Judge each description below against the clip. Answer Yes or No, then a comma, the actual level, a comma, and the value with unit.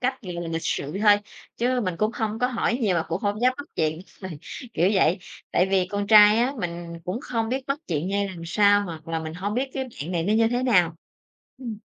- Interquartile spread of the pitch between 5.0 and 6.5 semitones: Yes, average, 5.3 semitones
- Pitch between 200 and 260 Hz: Yes, high, 205 Hz